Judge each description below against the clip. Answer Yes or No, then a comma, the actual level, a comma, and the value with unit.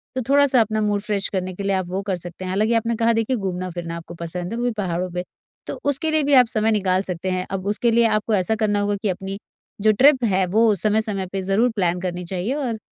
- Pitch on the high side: Yes, high, 205 Hz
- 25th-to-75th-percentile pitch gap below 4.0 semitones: Yes, average, 3.6 semitones